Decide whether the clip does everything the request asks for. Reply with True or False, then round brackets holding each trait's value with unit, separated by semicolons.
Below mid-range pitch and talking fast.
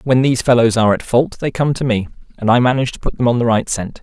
True (120 Hz; 300 wpm)